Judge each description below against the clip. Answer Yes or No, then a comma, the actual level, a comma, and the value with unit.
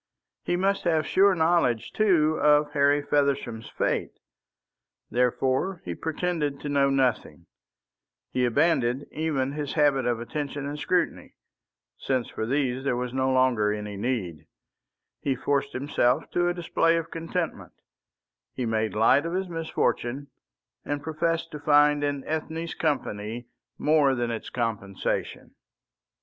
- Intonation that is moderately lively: Yes, average, 4.3 semitones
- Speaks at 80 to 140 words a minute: Yes, slow, 135 wpm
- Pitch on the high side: No, medium, 140 Hz